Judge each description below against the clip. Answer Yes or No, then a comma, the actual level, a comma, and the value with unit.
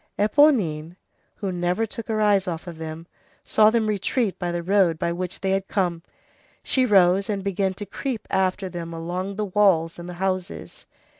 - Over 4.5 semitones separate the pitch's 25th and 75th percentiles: No, average, 3.1 semitones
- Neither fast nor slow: Yes, average, 180 wpm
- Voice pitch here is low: No, high, 190 Hz